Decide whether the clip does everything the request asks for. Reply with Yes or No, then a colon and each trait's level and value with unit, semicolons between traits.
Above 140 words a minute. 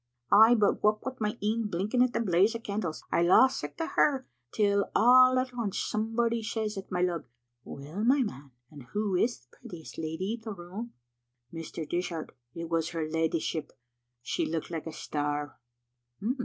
Yes: average, 180 wpm